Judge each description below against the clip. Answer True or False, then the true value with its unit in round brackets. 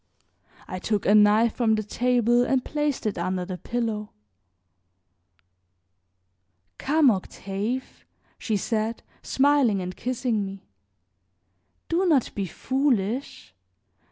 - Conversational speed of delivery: False (105 wpm)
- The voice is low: False (225 Hz)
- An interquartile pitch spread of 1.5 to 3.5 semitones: False (4.2 semitones)